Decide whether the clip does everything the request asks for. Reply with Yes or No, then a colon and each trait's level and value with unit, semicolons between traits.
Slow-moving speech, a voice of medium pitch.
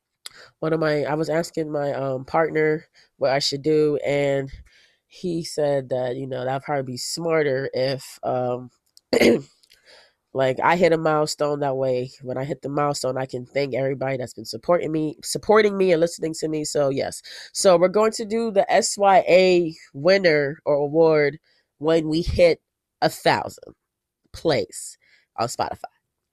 No: average, 160 wpm; medium, 150 Hz